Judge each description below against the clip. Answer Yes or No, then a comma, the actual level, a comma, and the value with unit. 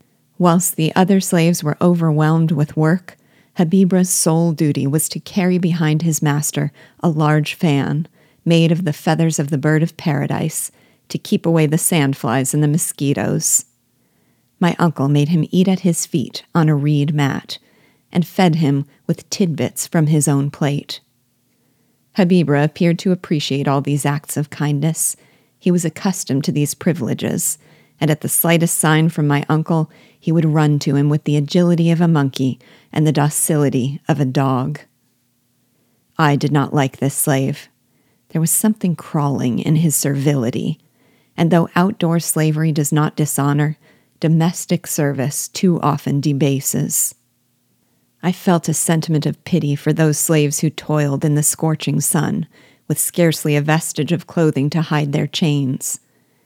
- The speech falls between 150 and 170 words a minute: Yes, average, 155 wpm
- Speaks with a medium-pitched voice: Yes, medium, 155 Hz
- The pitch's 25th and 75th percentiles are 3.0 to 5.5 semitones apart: No, narrow, 2.6 semitones